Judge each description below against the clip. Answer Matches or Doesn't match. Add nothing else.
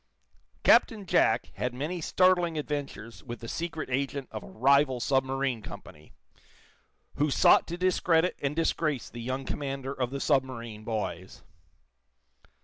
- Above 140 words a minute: Doesn't match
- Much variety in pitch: Doesn't match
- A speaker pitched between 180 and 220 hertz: Doesn't match